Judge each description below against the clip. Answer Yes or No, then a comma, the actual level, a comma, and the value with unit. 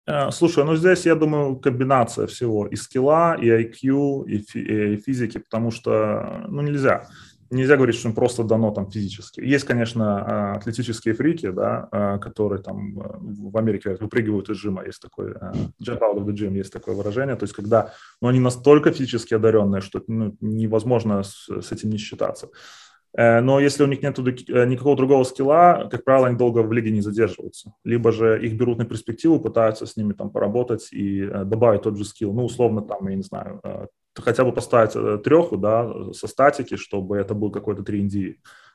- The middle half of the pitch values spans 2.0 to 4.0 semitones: Yes, average, 3.5 semitones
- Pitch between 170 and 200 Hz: No, low, 115 Hz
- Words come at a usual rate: No, fast, 175 wpm